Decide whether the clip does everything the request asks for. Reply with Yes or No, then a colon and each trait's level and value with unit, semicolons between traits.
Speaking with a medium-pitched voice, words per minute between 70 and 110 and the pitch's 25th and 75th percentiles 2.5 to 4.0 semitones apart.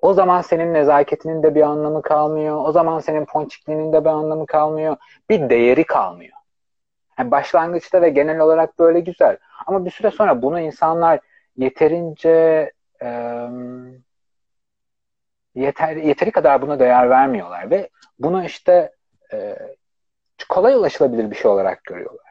No: medium, 155 Hz; average, 135 wpm; average, 2.8 semitones